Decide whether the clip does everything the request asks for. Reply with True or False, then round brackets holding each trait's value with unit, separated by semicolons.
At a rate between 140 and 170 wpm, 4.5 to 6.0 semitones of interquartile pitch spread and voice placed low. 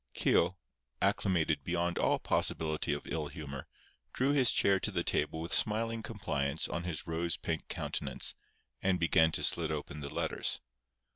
False (155 wpm; 3.7 semitones; 85 Hz)